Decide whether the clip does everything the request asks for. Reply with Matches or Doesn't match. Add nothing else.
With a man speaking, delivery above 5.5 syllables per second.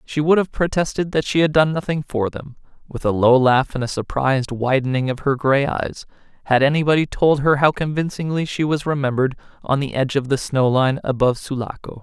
Matches